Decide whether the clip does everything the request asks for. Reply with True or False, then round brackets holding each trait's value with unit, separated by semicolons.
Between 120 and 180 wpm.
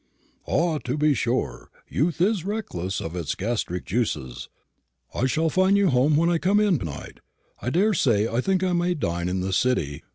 False (195 wpm)